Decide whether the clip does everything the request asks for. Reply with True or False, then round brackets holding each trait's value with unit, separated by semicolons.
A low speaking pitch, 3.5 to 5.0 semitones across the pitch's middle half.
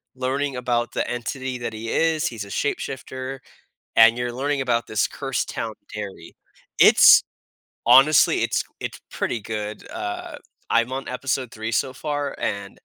False (125 Hz; 2.9 semitones)